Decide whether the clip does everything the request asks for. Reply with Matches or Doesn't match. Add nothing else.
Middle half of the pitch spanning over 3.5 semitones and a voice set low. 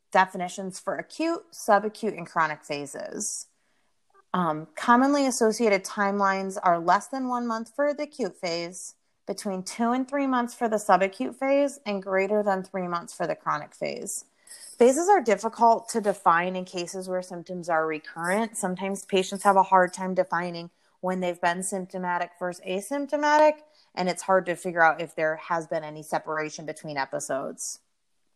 Doesn't match